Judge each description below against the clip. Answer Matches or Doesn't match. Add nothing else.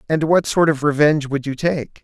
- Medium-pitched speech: Matches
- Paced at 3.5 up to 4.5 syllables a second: Doesn't match